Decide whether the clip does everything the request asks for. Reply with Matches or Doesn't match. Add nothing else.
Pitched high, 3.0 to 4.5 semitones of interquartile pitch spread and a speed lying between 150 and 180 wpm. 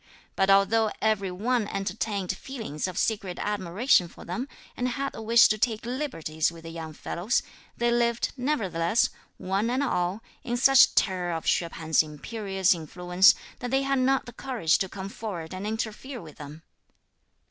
Doesn't match